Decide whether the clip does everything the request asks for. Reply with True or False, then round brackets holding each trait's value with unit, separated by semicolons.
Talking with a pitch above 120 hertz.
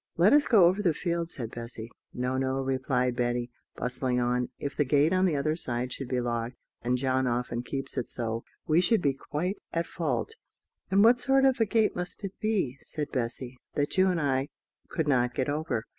True (135 Hz)